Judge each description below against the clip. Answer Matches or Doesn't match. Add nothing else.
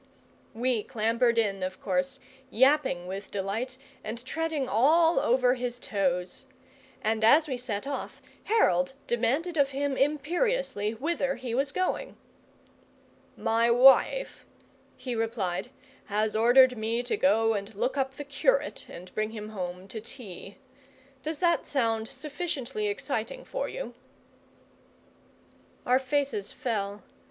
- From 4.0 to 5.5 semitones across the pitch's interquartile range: Matches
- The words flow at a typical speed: Doesn't match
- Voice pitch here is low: Doesn't match